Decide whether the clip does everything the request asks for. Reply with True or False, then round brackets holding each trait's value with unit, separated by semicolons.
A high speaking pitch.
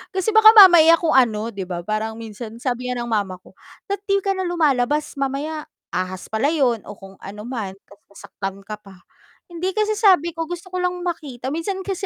True (280 Hz)